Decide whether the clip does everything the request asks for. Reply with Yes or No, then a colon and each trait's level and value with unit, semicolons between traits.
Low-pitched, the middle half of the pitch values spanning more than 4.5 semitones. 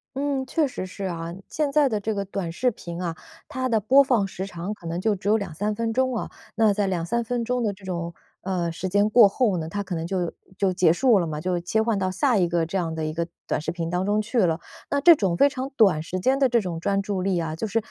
No: high, 195 Hz; average, 5.0 semitones